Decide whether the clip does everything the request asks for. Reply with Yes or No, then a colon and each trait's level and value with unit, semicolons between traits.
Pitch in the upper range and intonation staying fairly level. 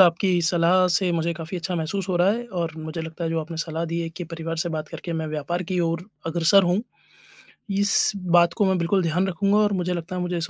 No: medium, 170 Hz; narrow, 2.1 semitones